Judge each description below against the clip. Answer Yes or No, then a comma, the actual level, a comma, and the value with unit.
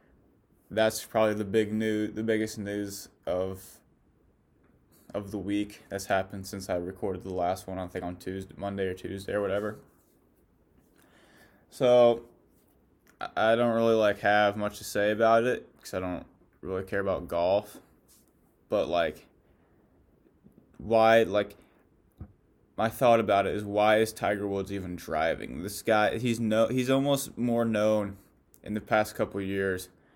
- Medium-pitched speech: No, low, 105 Hz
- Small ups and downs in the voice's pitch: Yes, narrow, 2.2 semitones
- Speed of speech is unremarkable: Yes, average, 150 wpm